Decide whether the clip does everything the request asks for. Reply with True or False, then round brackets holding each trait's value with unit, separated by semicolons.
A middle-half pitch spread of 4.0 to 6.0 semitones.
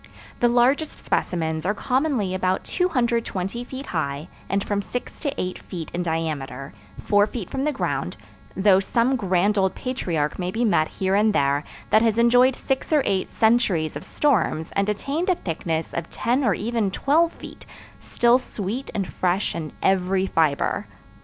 True (5.5 semitones)